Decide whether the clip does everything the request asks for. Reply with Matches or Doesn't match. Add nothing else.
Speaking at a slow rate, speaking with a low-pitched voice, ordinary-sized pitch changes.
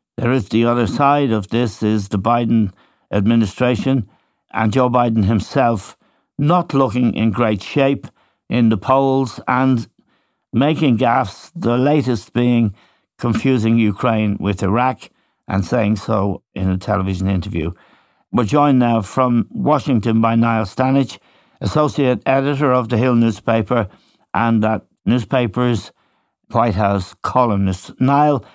Matches